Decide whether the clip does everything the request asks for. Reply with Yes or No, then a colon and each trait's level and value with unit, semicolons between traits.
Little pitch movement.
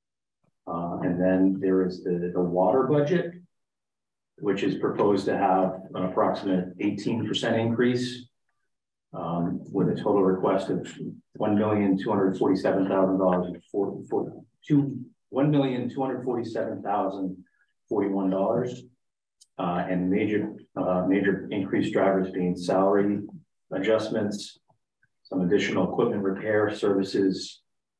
No: average, 3.6 semitones